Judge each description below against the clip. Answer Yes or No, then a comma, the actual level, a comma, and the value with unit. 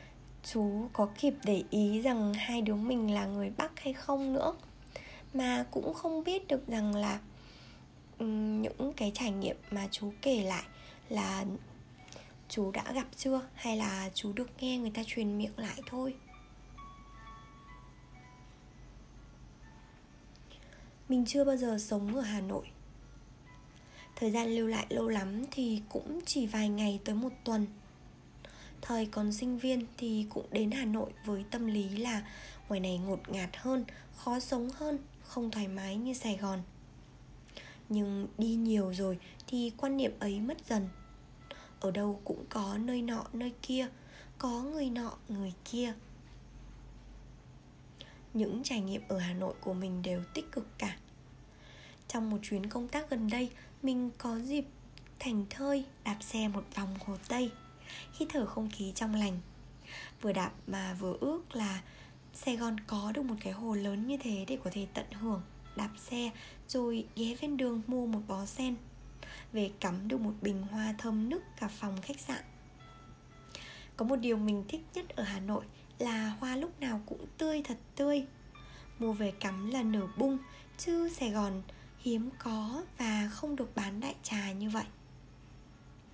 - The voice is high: Yes, high, 220 Hz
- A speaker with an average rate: No, slow, 160 wpm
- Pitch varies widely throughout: No, average, 3.8 semitones